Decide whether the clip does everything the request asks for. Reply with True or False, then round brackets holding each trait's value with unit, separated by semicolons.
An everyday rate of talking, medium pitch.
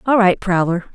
False (190 wpm; 195 Hz)